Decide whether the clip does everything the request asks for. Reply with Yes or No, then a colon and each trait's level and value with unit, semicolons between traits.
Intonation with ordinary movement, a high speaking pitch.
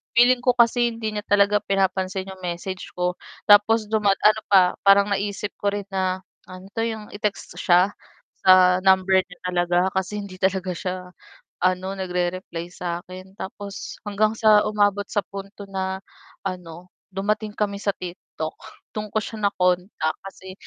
No: narrow, 2.1 semitones; high, 195 Hz